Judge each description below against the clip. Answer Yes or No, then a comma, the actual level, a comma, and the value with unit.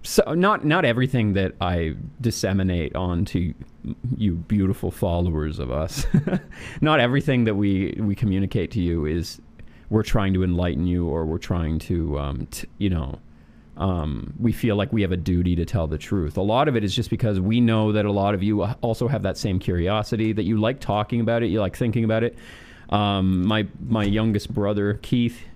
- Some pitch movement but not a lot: Yes, average, 4.5 semitones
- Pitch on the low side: Yes, low, 100 Hz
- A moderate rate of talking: Yes, average, 195 wpm